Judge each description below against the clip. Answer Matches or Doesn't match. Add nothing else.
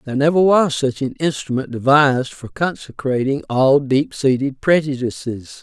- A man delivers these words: Matches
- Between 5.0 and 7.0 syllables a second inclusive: Doesn't match